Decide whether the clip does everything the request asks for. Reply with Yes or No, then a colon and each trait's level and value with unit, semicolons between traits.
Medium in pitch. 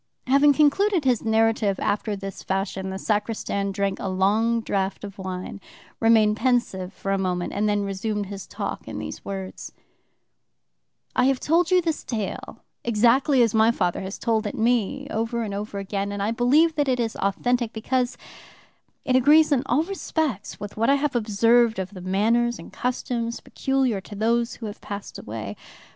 No: high, 220 Hz